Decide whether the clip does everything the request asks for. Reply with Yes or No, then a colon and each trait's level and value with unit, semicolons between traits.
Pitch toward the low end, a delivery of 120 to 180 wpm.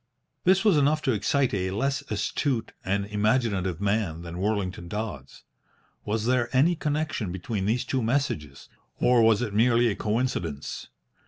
Yes: low, 110 Hz; average, 150 wpm